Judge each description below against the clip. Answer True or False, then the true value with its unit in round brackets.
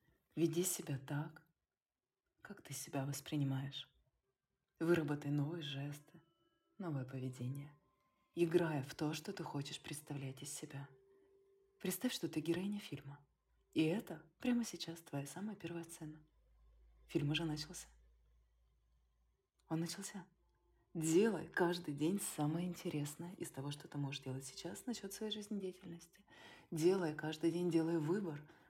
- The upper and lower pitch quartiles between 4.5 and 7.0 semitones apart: False (3.8 semitones)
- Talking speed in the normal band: True (125 wpm)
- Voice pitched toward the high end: False (160 Hz)